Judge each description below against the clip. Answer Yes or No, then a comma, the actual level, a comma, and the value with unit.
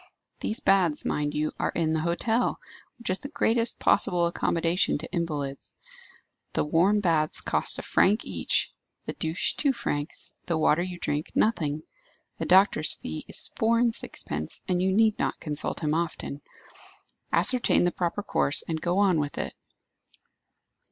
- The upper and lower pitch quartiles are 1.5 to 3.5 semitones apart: No, average, 4.6 semitones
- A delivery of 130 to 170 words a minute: Yes, average, 160 wpm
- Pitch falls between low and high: Yes, medium, 170 Hz